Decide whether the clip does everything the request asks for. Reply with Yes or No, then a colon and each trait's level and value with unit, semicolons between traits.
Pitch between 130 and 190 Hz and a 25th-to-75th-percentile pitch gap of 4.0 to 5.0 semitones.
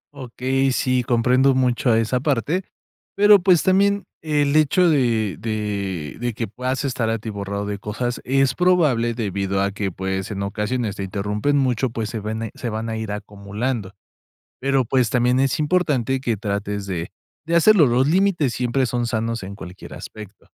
No: low, 120 Hz; average, 4.6 semitones